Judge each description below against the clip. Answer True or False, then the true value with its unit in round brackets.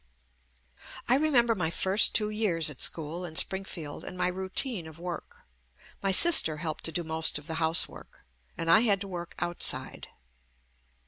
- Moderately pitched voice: True (175 Hz)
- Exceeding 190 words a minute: False (170 wpm)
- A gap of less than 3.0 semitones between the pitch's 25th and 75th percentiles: False (3.9 semitones)